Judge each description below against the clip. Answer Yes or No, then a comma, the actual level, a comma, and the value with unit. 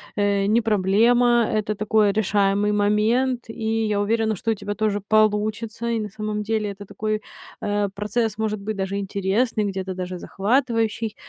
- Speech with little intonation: Yes, narrow, 1.6 semitones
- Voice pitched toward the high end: Yes, high, 210 Hz